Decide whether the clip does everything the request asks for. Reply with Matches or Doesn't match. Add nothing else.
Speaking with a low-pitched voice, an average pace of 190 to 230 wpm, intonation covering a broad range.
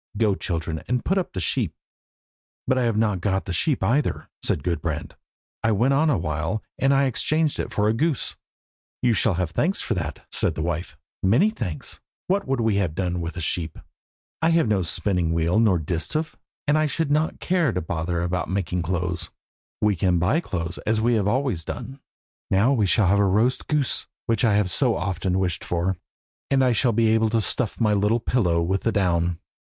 Matches